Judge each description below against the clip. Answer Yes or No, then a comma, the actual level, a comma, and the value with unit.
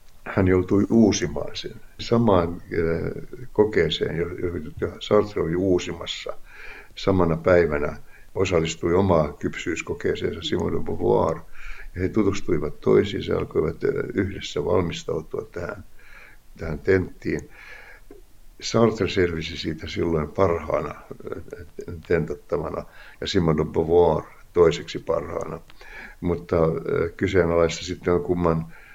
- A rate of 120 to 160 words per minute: No, slow, 95 wpm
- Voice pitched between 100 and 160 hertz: No, very low, 90 Hz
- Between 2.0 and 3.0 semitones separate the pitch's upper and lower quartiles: Yes, average, 2.7 semitones